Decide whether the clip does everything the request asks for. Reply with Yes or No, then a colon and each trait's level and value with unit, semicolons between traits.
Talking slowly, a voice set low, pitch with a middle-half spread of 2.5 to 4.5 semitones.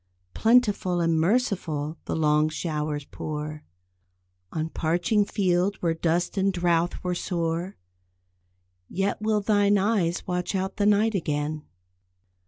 No: slow, 120 wpm; medium, 175 Hz; average, 4.0 semitones